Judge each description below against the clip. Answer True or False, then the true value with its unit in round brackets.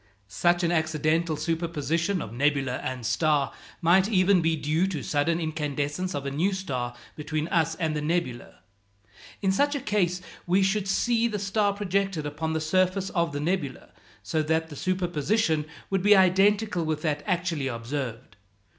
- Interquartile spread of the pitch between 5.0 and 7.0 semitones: False (4.3 semitones)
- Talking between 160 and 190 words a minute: True (165 wpm)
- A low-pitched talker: False (165 Hz)